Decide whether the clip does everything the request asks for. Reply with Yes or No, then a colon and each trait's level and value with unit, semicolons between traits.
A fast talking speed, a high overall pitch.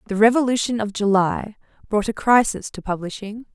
No: average, 150 wpm; high, 215 Hz